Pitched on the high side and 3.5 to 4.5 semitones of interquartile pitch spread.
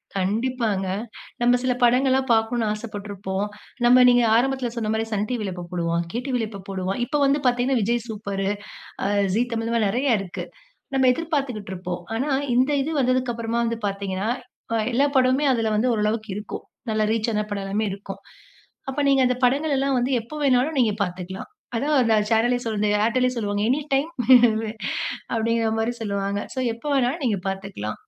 Yes: high, 230 Hz; average, 3.9 semitones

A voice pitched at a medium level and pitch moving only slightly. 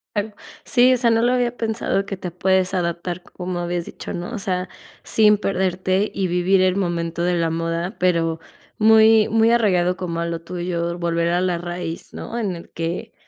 No: medium, 180 Hz; average, 3.4 semitones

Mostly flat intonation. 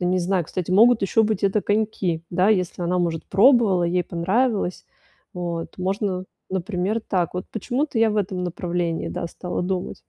No: average, 3.2 semitones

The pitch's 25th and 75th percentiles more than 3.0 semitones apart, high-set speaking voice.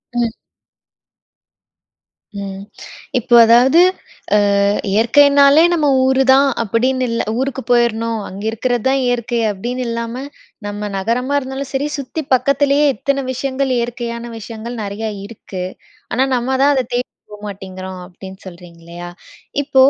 Yes: average, 4.0 semitones; high, 240 Hz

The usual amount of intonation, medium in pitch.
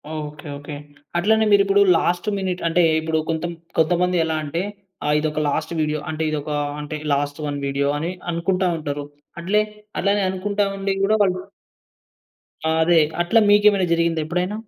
Yes: average, 3.9 semitones; medium, 170 Hz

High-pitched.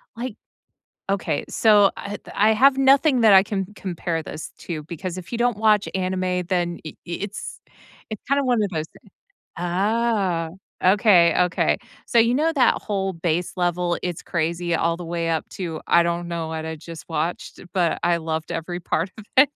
No: medium, 180 Hz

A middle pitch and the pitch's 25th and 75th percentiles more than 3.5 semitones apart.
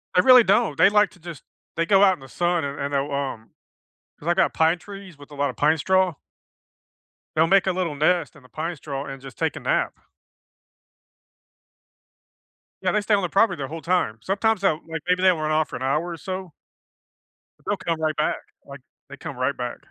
Yes: medium, 160 Hz; average, 4.6 semitones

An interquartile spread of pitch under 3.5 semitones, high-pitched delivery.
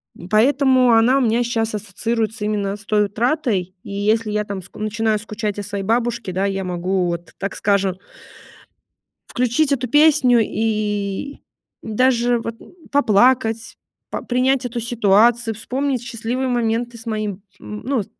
Yes: average, 3.0 semitones; high, 225 Hz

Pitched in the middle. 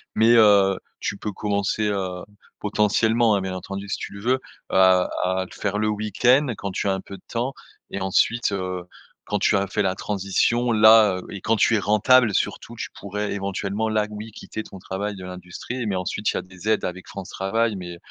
No: low, 100 Hz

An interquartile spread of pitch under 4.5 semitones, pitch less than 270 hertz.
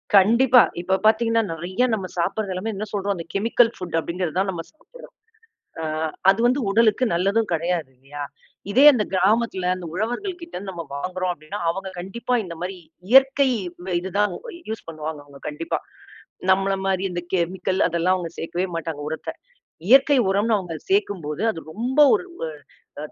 No: average, 4.8 semitones; high, 190 Hz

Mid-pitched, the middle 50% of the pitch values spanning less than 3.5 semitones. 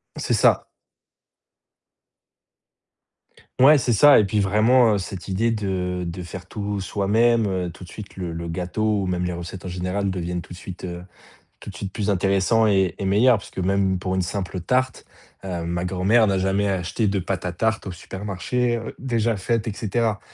No: very low, 95 Hz; average, 3.1 semitones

